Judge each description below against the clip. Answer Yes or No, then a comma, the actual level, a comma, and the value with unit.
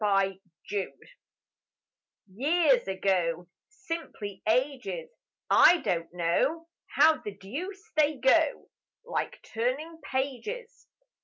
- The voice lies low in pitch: No, very high, 265 Hz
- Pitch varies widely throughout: Yes, wide, 8.9 semitones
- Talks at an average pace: No, slow, 85 wpm